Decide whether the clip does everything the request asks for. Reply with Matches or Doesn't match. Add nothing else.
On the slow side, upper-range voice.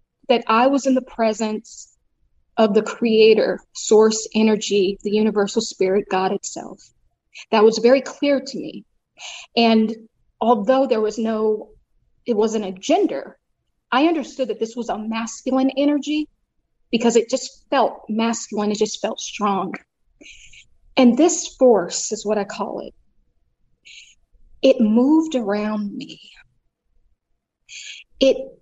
Matches